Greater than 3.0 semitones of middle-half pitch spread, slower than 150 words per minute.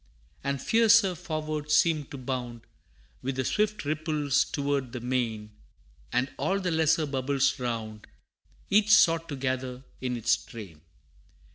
Yes: average, 4.4 semitones; slow, 135 wpm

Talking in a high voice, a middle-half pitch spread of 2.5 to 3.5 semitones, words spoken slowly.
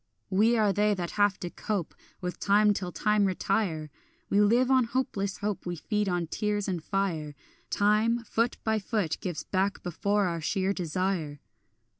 No: high, 200 Hz; average, 2.9 semitones; average, 165 wpm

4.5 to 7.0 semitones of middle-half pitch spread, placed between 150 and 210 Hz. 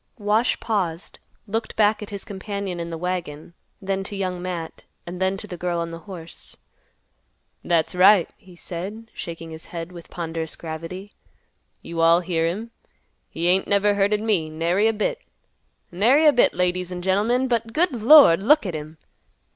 No: average, 3.7 semitones; medium, 185 Hz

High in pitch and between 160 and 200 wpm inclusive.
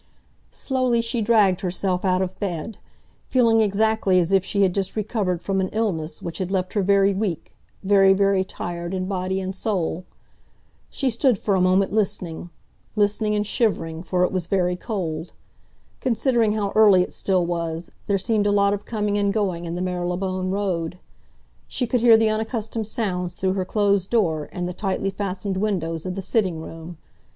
Yes: high, 195 Hz; average, 180 wpm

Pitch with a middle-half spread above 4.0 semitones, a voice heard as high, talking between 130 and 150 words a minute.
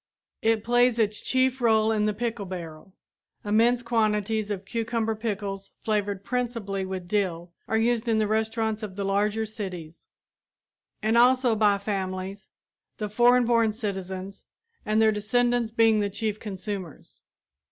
No: narrow, 2.4 semitones; high, 215 Hz; average, 140 wpm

